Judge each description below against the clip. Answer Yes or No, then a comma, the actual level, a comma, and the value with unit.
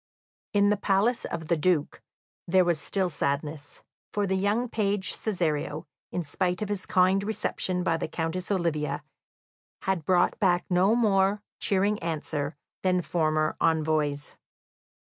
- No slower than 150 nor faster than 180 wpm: No, average, 140 wpm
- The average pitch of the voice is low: No, medium, 180 Hz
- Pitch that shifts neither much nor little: Yes, average, 3.9 semitones